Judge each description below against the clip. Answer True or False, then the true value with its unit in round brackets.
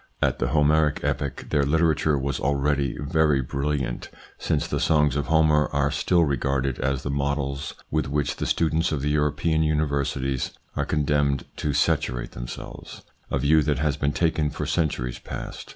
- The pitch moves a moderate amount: False (1.8 semitones)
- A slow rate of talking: False (165 wpm)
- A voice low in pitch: True (70 Hz)